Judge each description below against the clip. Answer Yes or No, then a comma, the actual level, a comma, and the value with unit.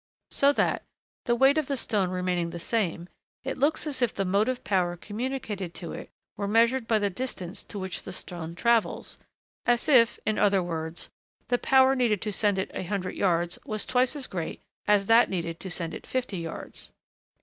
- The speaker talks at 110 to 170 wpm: No, average, 195 wpm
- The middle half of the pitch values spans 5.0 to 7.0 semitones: Yes, average, 5.3 semitones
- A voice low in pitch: No, high, 205 Hz